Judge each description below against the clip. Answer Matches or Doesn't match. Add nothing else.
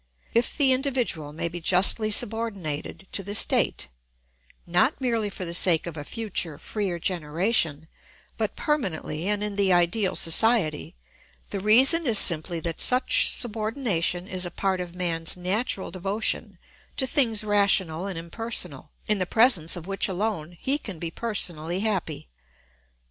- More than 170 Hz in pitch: Matches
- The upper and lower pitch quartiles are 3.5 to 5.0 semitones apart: Matches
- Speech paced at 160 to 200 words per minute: Doesn't match